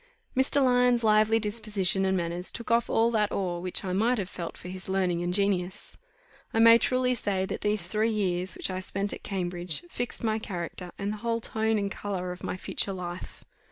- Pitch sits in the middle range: No, high, 200 Hz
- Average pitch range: Yes, average, 3.6 semitones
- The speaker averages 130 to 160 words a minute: No, fast, 205 wpm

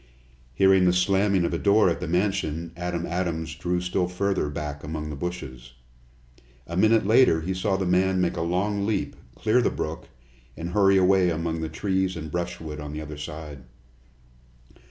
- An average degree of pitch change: Yes, average, 3.0 semitones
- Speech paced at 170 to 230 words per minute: Yes, average, 175 wpm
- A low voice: Yes, very low, 90 Hz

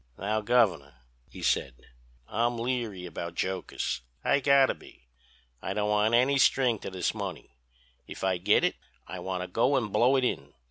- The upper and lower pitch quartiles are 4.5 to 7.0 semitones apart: Yes, wide, 5.4 semitones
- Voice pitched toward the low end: Yes, low, 105 Hz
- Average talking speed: Yes, average, 170 wpm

